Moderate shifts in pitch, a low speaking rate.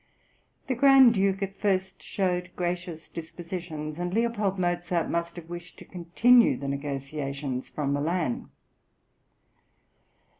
Yes: average, 3.8 semitones; slow, 115 wpm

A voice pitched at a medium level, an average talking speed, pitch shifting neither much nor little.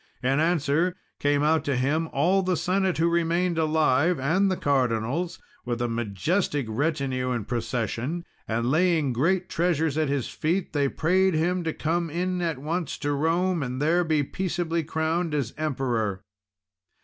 Yes: medium, 155 Hz; average, 160 wpm; average, 4.3 semitones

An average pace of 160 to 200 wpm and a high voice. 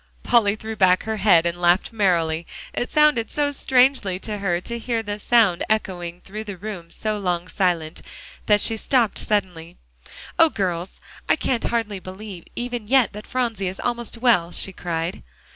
Yes: average, 170 wpm; high, 205 Hz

